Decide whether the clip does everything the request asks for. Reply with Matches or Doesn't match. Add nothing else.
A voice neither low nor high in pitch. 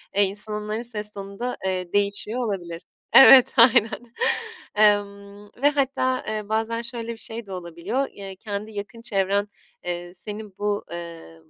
Doesn't match